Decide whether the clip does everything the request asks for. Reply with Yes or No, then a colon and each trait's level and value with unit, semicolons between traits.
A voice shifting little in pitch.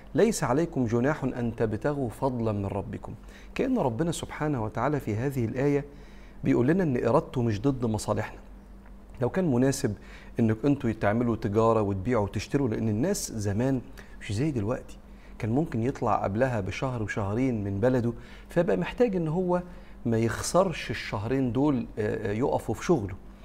No: average, 4.3 semitones